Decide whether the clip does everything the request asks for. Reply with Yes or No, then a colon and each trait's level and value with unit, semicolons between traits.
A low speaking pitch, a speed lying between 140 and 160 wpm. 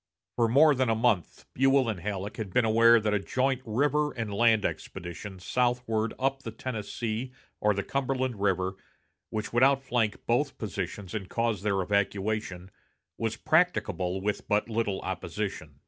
Yes: low, 110 Hz; average, 155 wpm